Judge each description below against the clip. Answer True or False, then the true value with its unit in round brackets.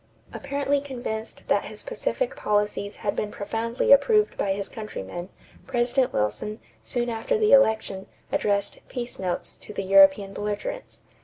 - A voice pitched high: True (220 Hz)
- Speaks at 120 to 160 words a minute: True (145 wpm)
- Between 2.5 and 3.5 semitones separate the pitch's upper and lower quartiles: False (5.1 semitones)